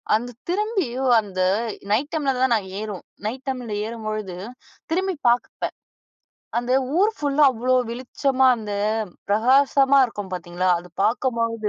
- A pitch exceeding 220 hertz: Yes, high, 245 Hz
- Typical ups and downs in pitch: Yes, average, 4.2 semitones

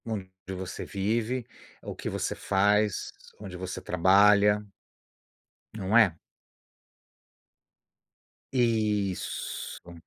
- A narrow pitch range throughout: Yes, narrow, 2.3 semitones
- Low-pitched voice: Yes, low, 105 Hz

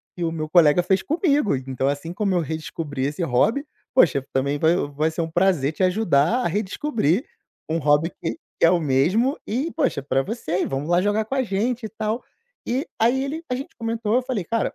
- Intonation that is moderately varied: No, wide, 7.2 semitones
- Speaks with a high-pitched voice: No, medium, 180 Hz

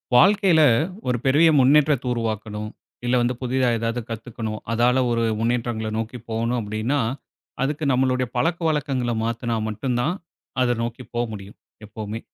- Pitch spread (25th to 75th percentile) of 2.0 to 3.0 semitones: Yes, average, 2.7 semitones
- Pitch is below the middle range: Yes, low, 120 Hz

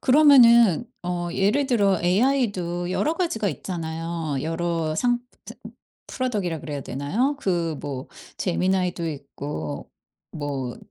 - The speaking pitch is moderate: Yes, medium, 175 Hz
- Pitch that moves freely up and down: Yes, wide, 6.5 semitones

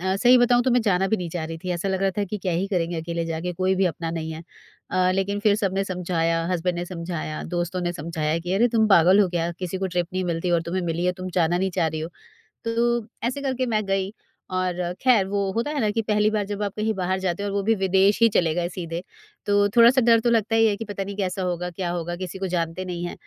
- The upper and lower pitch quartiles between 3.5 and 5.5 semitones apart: No, average, 3.1 semitones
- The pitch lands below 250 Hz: Yes, medium, 185 Hz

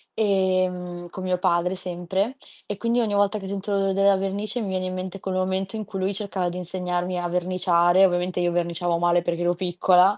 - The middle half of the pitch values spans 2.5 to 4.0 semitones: No, narrow, 1.7 semitones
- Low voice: No, medium, 185 Hz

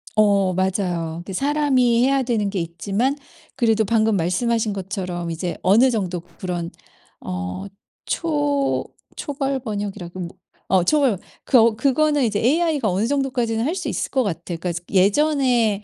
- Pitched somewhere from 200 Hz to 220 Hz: Yes, high, 215 Hz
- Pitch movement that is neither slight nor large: No, wide, 6.3 semitones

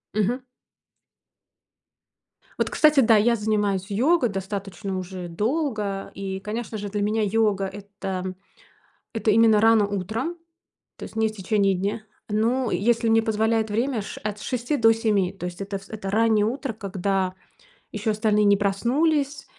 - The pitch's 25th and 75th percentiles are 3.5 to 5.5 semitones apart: No, narrow, 2.4 semitones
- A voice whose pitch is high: Yes, high, 210 Hz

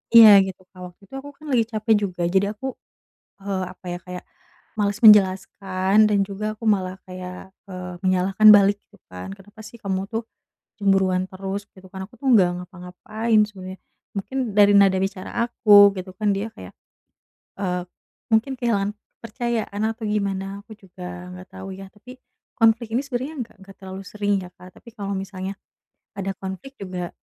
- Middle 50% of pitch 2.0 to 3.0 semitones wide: Yes, narrow, 2.4 semitones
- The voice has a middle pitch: No, high, 200 Hz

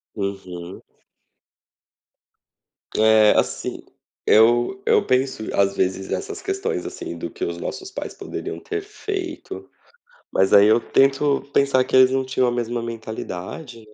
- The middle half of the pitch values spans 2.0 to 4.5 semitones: No, wide, 5.5 semitones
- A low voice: Yes, low, 120 Hz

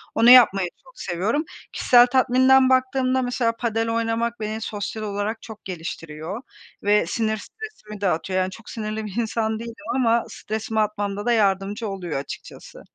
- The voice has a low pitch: No, high, 220 Hz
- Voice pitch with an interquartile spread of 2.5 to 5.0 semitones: Yes, average, 2.8 semitones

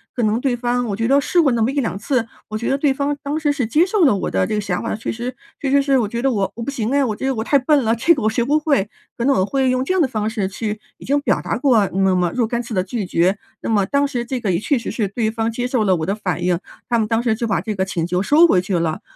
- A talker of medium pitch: No, high, 235 Hz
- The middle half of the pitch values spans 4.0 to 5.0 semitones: Yes, average, 4.6 semitones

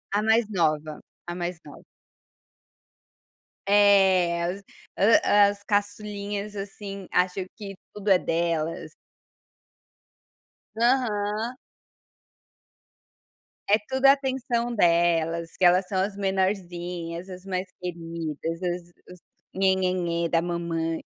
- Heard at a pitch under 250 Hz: Yes, medium, 185 Hz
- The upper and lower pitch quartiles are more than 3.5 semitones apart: No, average, 3.1 semitones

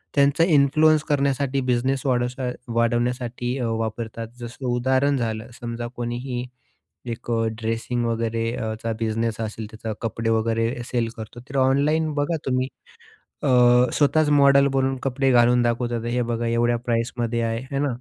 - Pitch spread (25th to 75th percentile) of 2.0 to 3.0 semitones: Yes, average, 2.7 semitones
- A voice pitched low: Yes, low, 120 Hz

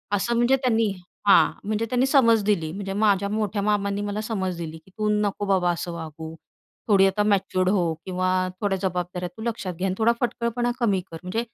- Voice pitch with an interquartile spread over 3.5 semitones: No, average, 3.0 semitones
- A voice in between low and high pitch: No, high, 200 Hz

